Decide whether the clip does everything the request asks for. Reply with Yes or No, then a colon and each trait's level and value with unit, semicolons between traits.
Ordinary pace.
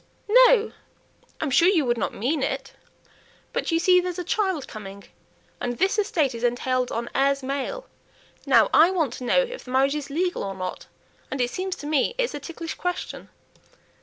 Yes: average, 190 wpm